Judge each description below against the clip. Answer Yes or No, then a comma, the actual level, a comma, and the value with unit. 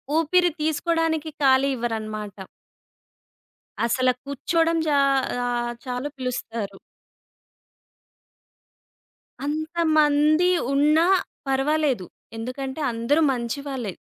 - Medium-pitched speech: No, very high, 275 Hz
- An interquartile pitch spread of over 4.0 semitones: Yes, average, 4.7 semitones